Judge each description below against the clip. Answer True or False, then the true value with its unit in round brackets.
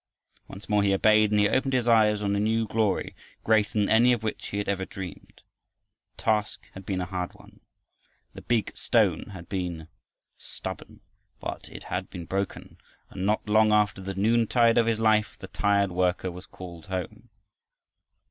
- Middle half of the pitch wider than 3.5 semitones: False (2.5 semitones)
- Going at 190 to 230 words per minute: False (180 wpm)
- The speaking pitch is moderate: False (105 Hz)